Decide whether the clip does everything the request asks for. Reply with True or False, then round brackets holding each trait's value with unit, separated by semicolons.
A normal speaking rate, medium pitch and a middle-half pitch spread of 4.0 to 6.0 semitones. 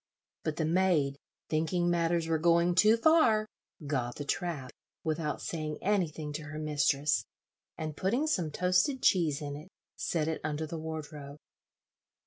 False (145 wpm; 160 Hz; 2.9 semitones)